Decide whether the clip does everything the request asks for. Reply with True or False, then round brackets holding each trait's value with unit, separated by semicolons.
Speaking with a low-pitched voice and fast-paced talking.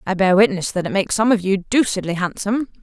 False (195 Hz; 235 wpm)